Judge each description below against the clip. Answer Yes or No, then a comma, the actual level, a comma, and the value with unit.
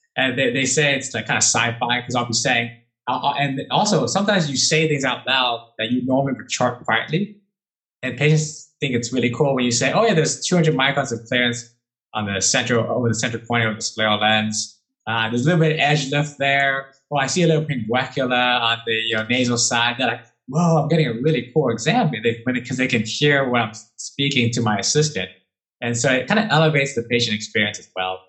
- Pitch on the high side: No, low, 125 Hz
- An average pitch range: Yes, average, 3.8 semitones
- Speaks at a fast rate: Yes, fast, 230 wpm